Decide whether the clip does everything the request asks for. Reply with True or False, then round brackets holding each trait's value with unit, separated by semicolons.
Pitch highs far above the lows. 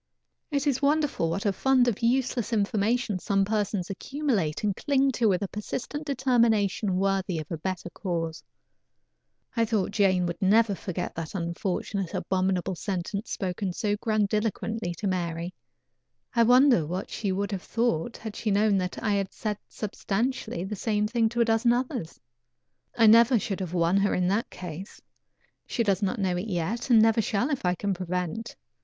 False (3.9 semitones)